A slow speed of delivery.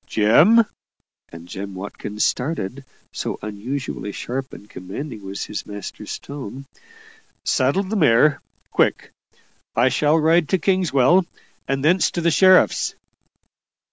Yes: slow, 120 wpm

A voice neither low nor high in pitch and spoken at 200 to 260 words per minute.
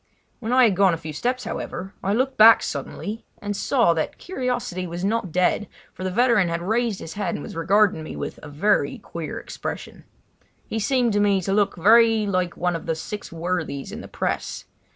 No: high, 200 Hz; fast, 205 wpm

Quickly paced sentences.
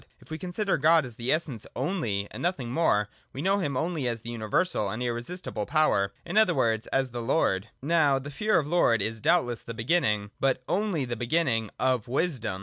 Yes: fast, 210 wpm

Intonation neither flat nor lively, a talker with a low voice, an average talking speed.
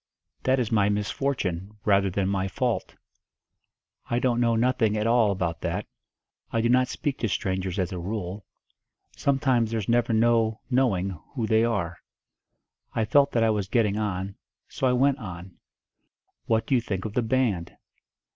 Yes: average, 3.7 semitones; low, 110 Hz; average, 165 wpm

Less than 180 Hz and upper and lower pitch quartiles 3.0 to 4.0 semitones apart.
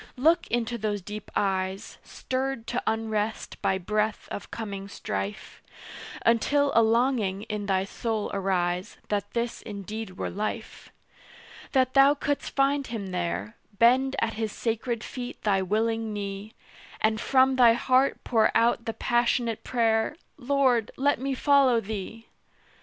No: high, 225 Hz; average, 3.5 semitones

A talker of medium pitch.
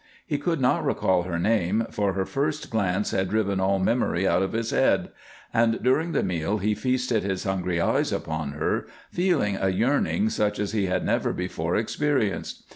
No: low, 105 Hz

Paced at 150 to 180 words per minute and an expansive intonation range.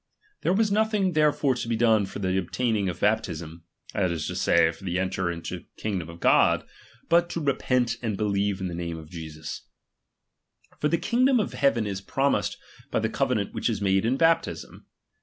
No: average, 195 wpm; wide, 8.2 semitones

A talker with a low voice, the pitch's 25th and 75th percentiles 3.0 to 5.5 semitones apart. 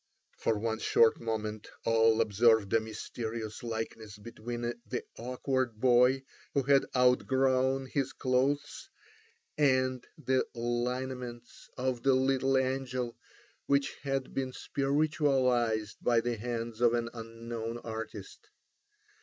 No: low, 120 Hz; narrow, 2.5 semitones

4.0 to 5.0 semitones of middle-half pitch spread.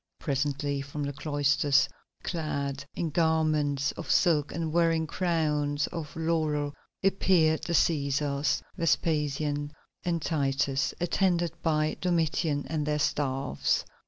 No: narrow, 2.4 semitones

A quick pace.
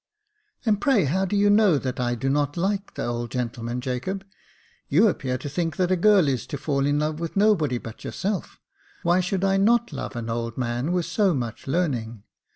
Yes: fast, 210 wpm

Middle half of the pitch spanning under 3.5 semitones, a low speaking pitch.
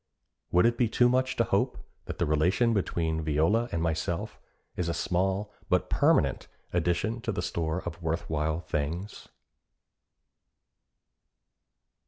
No: average, 5.3 semitones; very low, 85 Hz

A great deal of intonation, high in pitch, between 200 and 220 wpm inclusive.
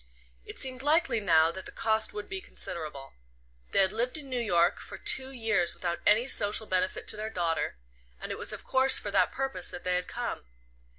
Yes: wide, 6.0 semitones; high, 210 Hz; fast, 205 wpm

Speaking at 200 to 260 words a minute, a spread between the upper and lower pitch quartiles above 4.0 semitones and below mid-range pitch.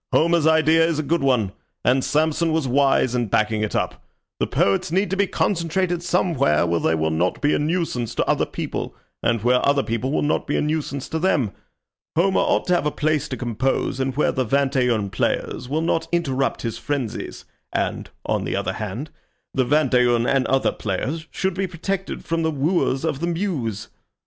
No: fast, 205 wpm; average, 5.0 semitones; medium, 145 Hz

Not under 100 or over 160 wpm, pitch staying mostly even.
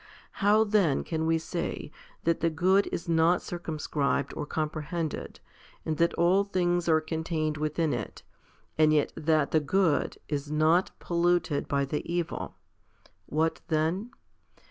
Yes: average, 145 wpm; narrow, 2.2 semitones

